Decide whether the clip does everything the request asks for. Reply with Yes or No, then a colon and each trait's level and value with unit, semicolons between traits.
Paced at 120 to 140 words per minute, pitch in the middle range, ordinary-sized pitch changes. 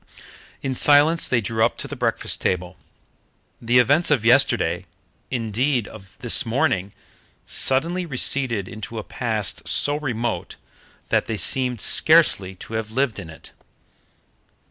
No: slow, 135 wpm; low, 120 Hz; average, 4.3 semitones